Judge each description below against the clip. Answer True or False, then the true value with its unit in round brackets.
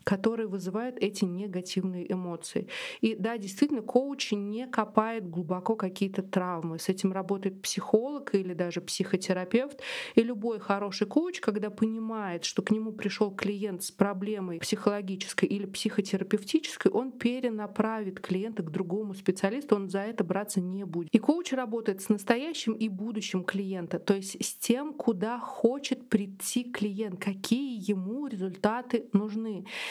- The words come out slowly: False (140 wpm)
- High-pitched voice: True (210 Hz)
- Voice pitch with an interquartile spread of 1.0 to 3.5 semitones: True (2.9 semitones)